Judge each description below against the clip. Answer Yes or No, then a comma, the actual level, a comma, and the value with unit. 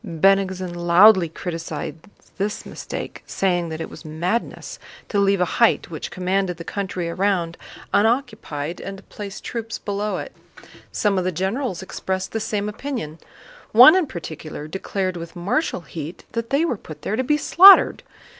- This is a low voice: No, high, 190 Hz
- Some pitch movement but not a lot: Yes, average, 4.0 semitones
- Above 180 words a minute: No, average, 160 wpm